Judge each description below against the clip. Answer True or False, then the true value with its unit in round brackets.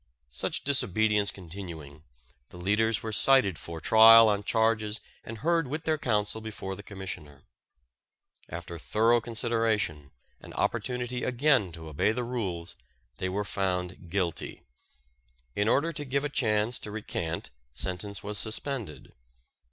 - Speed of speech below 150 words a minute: True (135 wpm)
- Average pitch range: True (4.3 semitones)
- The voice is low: True (105 Hz)